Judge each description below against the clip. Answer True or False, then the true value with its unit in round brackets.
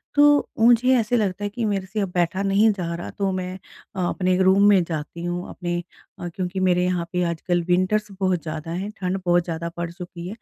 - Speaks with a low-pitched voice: False (185 Hz)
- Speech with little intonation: True (2.3 semitones)